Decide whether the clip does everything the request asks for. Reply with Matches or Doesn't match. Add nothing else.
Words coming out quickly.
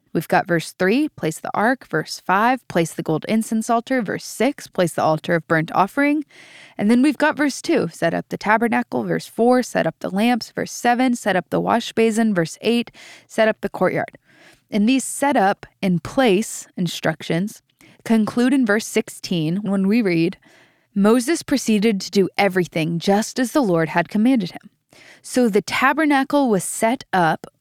Doesn't match